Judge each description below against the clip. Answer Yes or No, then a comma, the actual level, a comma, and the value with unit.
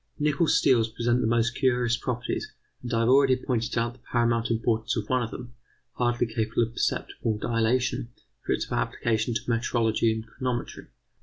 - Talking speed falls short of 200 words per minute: Yes, average, 170 wpm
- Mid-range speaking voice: No, low, 120 Hz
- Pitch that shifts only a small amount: Yes, narrow, 1.5 semitones